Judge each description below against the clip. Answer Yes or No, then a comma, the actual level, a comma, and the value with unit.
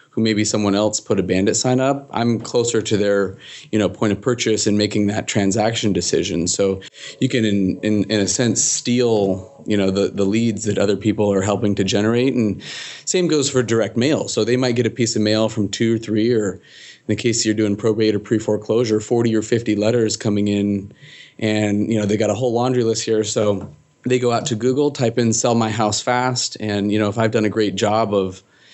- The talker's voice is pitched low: Yes, low, 110 Hz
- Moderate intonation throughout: No, narrow, 2.3 semitones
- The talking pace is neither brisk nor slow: No, fast, 230 wpm